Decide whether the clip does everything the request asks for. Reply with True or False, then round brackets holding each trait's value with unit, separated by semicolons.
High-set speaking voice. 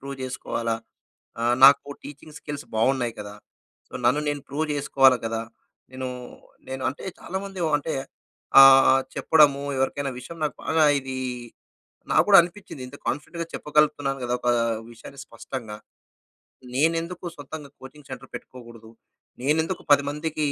False (140 Hz)